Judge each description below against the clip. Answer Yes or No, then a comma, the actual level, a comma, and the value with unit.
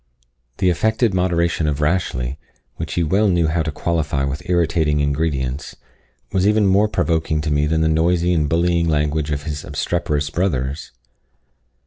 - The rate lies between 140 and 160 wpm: Yes, average, 155 wpm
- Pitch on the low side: Yes, very low, 80 Hz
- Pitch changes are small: No, average, 3.0 semitones